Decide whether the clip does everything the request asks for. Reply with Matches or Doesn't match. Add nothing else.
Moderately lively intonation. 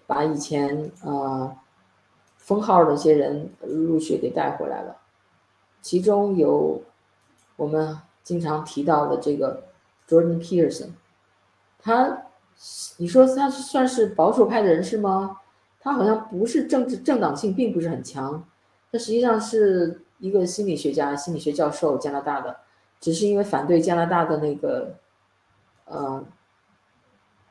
Doesn't match